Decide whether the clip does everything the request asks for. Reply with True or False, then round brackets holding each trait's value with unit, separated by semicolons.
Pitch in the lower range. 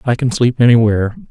True (120 Hz)